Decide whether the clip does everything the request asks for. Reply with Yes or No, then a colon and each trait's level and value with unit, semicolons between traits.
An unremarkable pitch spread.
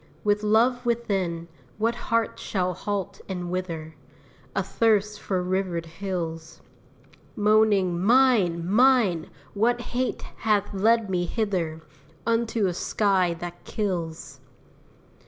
Yes: average, 4.0 semitones